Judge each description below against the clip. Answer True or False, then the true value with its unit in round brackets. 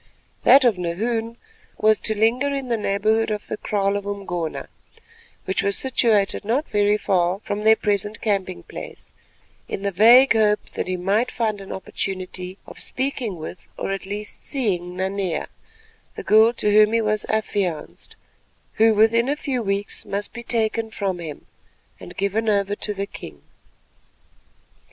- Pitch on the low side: False (210 Hz)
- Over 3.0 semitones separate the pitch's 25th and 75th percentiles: False (2.4 semitones)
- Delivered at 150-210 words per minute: True (160 wpm)